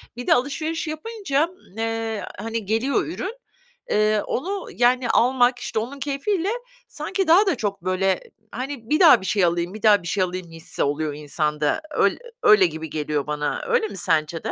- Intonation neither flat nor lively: No, wide, 8.9 semitones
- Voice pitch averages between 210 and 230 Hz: Yes, high, 225 Hz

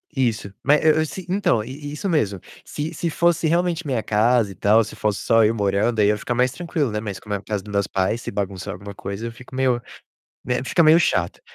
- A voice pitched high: No, low, 115 Hz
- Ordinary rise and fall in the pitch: No, wide, 6.6 semitones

